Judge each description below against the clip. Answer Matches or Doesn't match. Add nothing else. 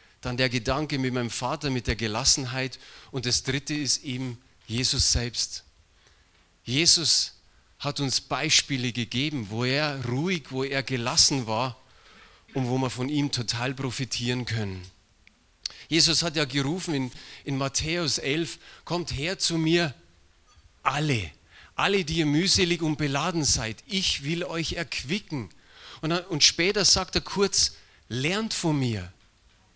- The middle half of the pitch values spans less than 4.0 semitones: Doesn't match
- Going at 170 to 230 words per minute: Doesn't match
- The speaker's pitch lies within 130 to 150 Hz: Matches